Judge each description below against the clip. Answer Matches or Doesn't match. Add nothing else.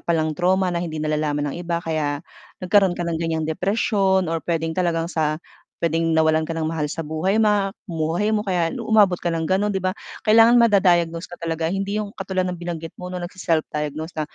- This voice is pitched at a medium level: Matches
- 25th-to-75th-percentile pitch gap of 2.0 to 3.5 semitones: Matches